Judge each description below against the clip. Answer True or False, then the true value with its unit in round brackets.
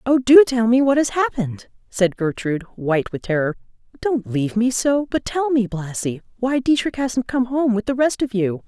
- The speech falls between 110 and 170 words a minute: False (205 wpm)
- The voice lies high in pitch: True (235 Hz)